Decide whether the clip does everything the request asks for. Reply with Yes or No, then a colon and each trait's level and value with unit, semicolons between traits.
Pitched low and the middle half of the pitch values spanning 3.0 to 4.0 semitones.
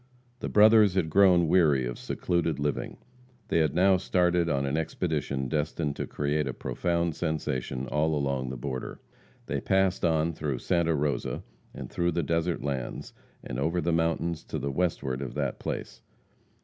Yes: very low, 80 Hz; average, 3.7 semitones